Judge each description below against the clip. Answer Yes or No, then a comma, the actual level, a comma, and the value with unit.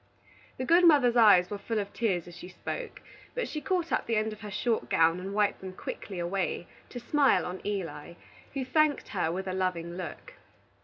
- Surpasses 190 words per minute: Yes, fast, 205 wpm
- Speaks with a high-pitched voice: Yes, high, 205 Hz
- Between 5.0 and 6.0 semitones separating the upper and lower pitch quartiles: Yes, wide, 5.4 semitones